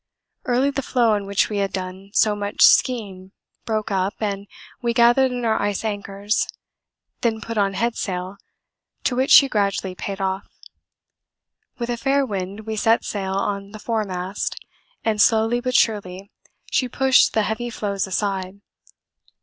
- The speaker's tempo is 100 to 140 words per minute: No, average, 160 wpm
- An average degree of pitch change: Yes, average, 3.1 semitones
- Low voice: No, high, 210 Hz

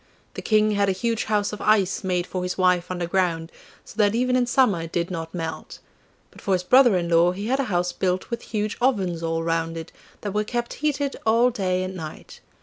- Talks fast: Yes, fast, 225 wpm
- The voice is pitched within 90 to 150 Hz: No, high, 190 Hz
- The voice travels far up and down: No, average, 4.0 semitones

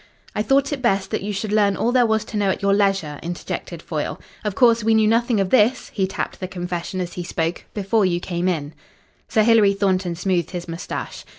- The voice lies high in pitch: Yes, high, 195 Hz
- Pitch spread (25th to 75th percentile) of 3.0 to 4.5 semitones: Yes, average, 3.5 semitones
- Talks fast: Yes, fast, 220 wpm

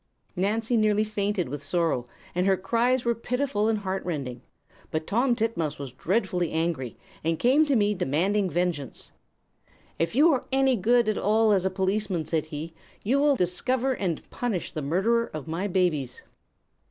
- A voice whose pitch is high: Yes, high, 195 Hz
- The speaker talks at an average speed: Yes, average, 165 wpm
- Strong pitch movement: Yes, wide, 5.7 semitones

